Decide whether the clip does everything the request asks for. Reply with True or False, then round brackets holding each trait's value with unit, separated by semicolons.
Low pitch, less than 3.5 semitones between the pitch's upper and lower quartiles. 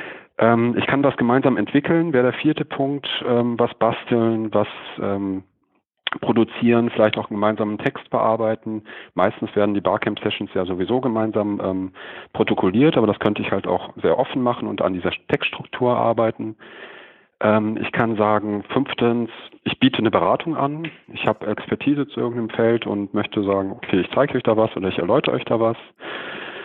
True (115 Hz; 2.5 semitones)